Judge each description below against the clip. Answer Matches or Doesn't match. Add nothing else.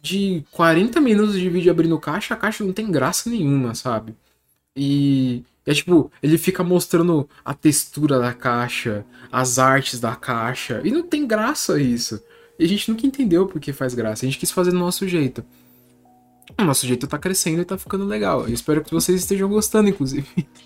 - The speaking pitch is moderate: Matches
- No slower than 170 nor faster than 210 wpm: Matches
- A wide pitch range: Matches